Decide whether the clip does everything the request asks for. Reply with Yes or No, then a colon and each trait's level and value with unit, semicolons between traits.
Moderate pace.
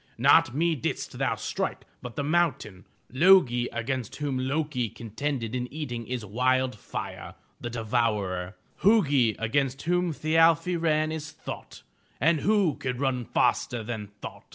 Yes: average, 145 wpm